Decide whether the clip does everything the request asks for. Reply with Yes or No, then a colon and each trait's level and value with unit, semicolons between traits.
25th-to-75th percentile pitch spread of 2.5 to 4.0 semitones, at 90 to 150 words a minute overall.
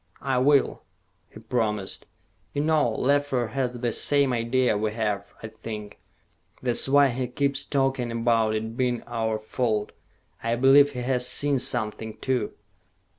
Yes: average, 3.2 semitones; average, 145 wpm